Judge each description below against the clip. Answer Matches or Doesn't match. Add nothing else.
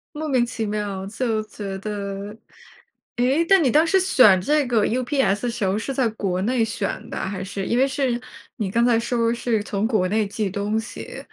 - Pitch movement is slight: Doesn't match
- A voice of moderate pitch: Doesn't match